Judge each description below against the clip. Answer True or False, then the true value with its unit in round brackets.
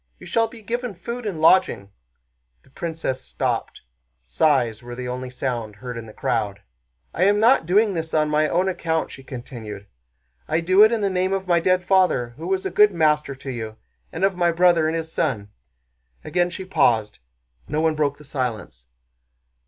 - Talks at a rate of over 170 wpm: True (190 wpm)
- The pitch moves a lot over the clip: True (6.9 semitones)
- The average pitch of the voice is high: False (160 Hz)